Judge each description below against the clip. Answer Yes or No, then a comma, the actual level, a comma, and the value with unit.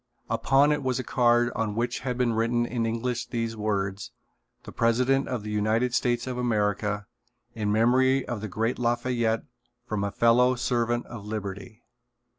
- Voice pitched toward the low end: Yes, low, 120 Hz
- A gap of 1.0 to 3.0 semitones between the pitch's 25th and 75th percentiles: Yes, narrow, 2.4 semitones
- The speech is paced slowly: No, average, 165 wpm